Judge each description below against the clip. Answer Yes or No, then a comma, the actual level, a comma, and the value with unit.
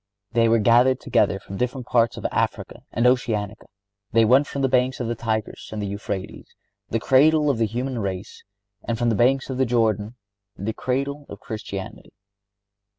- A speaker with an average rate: Yes, average, 175 wpm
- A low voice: Yes, low, 120 Hz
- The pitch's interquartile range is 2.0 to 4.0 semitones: Yes, average, 3.1 semitones